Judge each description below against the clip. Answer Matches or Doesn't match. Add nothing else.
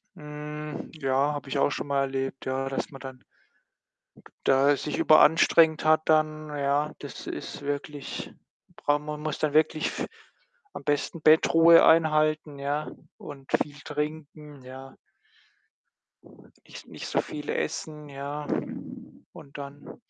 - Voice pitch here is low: Doesn't match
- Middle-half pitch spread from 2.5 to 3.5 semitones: Doesn't match